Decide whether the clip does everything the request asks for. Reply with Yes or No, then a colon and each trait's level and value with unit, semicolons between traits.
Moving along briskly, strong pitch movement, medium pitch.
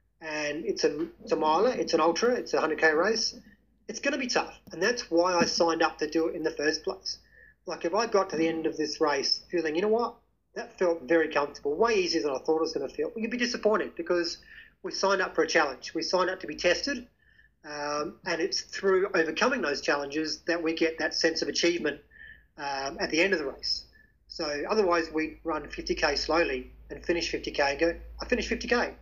Yes: fast, 225 wpm; wide, 6.4 semitones; medium, 170 Hz